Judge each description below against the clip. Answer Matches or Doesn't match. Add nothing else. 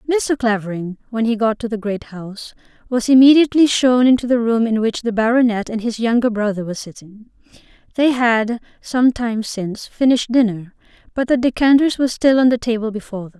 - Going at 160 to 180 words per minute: Doesn't match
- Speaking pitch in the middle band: Doesn't match